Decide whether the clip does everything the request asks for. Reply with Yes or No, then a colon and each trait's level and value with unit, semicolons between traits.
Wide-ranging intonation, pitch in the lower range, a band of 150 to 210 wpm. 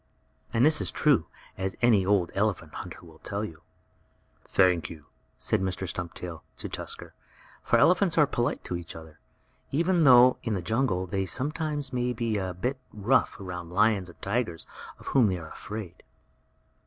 Yes: wide, 5.9 semitones; low, 100 Hz; average, 165 wpm